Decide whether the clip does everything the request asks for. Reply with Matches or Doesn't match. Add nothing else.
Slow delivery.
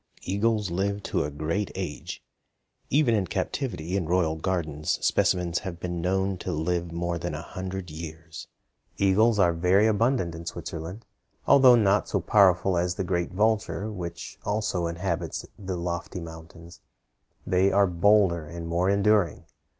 Doesn't match